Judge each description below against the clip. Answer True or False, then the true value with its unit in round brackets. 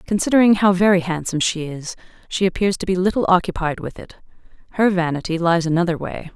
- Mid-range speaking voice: True (180 Hz)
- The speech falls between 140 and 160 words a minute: False (180 wpm)